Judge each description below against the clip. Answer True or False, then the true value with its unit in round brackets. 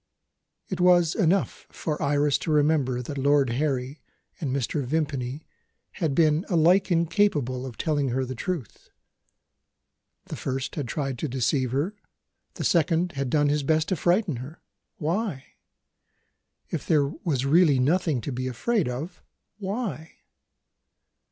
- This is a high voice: False (150 Hz)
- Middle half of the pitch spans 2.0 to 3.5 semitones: False (4.3 semitones)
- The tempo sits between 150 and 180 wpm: False (140 wpm)